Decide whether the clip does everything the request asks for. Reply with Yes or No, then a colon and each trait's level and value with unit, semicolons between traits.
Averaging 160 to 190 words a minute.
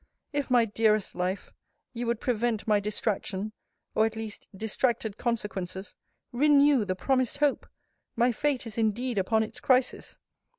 No: average, 140 wpm